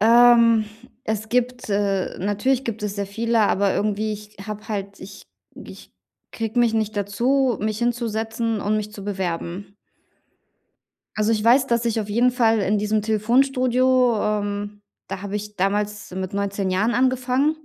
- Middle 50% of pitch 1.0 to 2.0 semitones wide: No, average, 2.7 semitones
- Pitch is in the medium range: No, high, 215 Hz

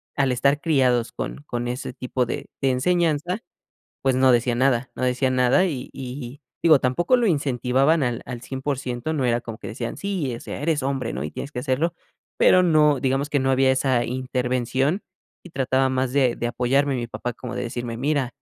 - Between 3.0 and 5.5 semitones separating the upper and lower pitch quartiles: No, narrow, 2.6 semitones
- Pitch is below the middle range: Yes, low, 130 Hz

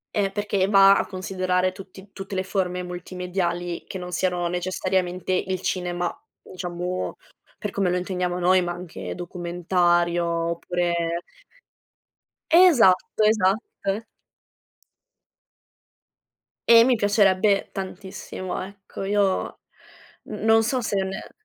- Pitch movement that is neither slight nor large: No, narrow, 1.8 semitones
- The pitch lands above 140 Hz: Yes, medium, 185 Hz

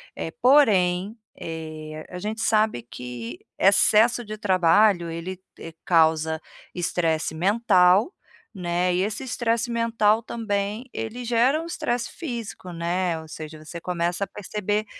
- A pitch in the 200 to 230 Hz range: No, high, 190 Hz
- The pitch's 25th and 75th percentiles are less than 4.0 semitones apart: No, average, 5.1 semitones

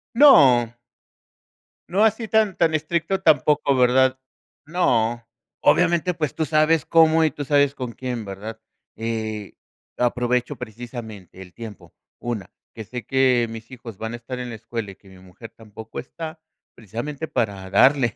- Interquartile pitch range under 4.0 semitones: No, wide, 5.4 semitones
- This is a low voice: Yes, low, 125 Hz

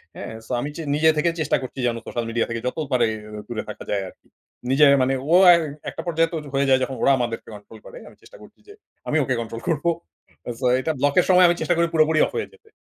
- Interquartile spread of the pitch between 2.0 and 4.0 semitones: No, wide, 5.5 semitones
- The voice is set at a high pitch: No, medium, 140 Hz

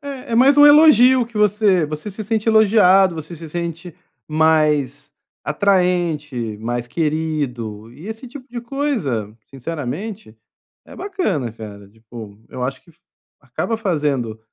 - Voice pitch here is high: No, medium, 165 Hz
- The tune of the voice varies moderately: No, wide, 9.0 semitones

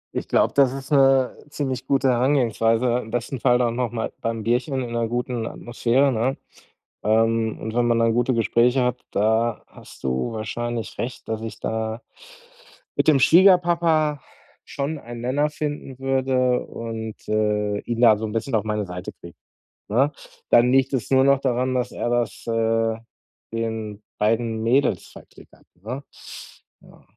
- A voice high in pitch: No, low, 120 Hz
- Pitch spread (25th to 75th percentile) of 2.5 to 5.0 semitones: Yes, average, 2.9 semitones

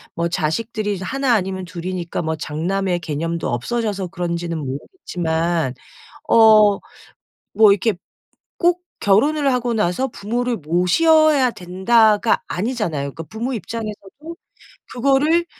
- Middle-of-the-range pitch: No, high, 200 Hz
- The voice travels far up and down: Yes, wide, 5.9 semitones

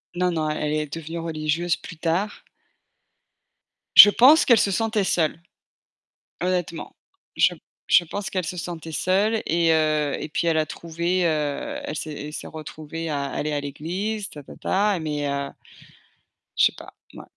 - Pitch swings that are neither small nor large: Yes, average, 3.3 semitones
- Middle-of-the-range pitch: Yes, medium, 165 Hz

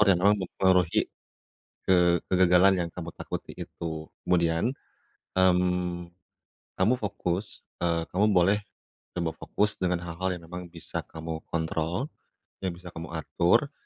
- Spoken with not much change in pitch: Yes, narrow, 1.9 semitones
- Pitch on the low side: Yes, very low, 90 Hz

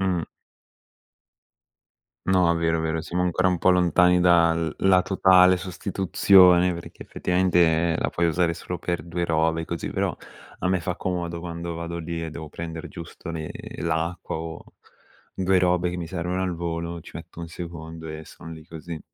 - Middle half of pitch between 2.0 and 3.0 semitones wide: No, narrow, 1.5 semitones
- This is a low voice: Yes, very low, 85 Hz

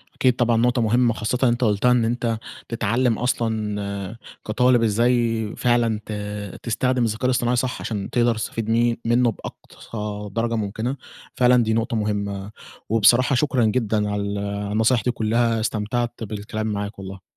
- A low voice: Yes, low, 115 Hz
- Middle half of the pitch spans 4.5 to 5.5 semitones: No, narrow, 2.4 semitones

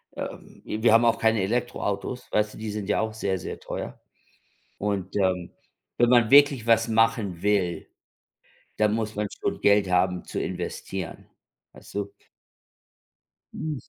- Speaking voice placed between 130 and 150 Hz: No, low, 105 Hz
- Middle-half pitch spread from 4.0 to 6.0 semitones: No, average, 2.8 semitones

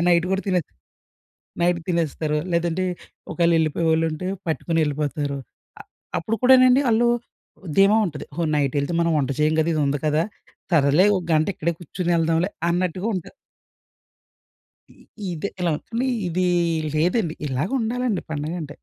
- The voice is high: No, medium, 170 Hz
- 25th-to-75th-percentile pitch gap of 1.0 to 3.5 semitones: Yes, average, 3.1 semitones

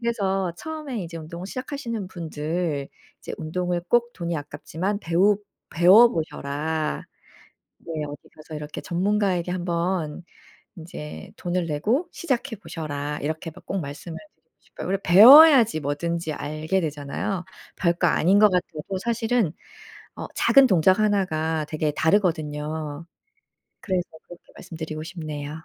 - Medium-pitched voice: Yes, medium, 170 Hz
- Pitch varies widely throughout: No, average, 4.2 semitones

